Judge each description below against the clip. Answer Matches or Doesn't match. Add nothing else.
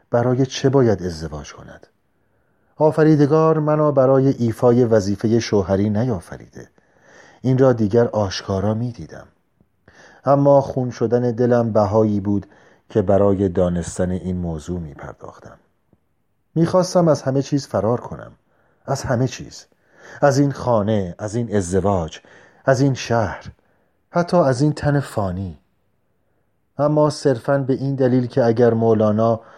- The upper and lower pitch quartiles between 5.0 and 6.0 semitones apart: Matches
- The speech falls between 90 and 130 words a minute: Matches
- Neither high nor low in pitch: Doesn't match